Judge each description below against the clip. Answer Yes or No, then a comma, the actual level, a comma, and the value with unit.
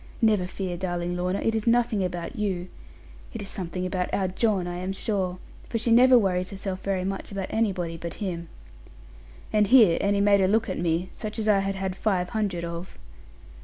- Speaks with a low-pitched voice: No, high, 190 Hz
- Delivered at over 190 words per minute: Yes, average, 200 wpm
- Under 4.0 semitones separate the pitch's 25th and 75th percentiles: Yes, average, 2.8 semitones